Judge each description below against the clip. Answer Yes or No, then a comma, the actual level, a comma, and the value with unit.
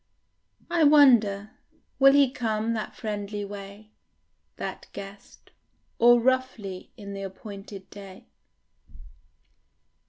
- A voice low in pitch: No, high, 210 Hz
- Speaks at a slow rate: Yes, slow, 95 wpm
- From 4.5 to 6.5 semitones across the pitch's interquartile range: No, average, 3.3 semitones